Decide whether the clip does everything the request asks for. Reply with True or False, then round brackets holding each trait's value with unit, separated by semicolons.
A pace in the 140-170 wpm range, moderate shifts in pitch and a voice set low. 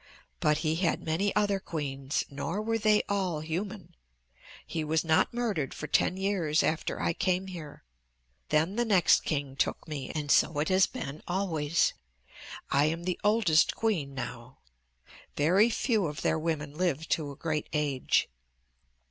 False (155 wpm; 4.3 semitones; 160 Hz)